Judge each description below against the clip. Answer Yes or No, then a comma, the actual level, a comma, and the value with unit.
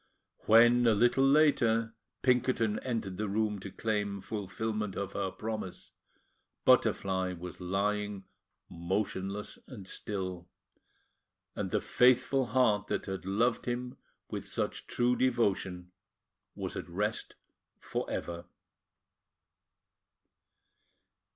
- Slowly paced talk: Yes, slow, 105 wpm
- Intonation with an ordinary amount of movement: Yes, average, 3.6 semitones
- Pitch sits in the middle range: No, low, 105 Hz